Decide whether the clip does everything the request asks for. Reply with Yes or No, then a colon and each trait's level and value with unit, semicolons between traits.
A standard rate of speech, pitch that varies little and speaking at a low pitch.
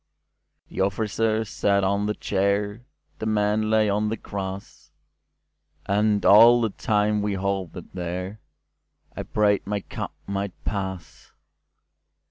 No: slow, 105 wpm; narrow, 1.6 semitones; low, 105 Hz